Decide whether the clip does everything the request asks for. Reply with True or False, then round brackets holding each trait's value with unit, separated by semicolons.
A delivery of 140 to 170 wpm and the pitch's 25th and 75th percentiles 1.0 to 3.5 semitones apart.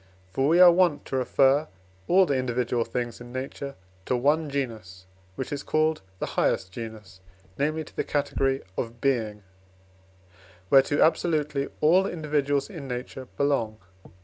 False (145 wpm; 3.9 semitones)